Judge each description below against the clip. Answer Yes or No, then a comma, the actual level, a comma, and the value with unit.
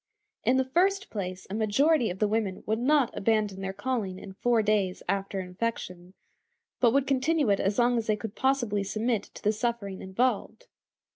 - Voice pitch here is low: No, high, 220 Hz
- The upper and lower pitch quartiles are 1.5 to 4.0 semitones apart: No, average, 4.4 semitones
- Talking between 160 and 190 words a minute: Yes, average, 185 wpm